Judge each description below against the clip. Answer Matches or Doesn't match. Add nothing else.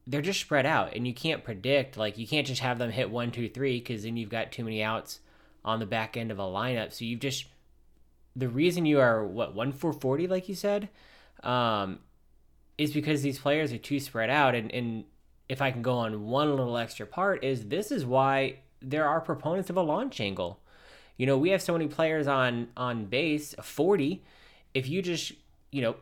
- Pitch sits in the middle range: Doesn't match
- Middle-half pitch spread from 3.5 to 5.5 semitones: Matches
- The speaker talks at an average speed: Doesn't match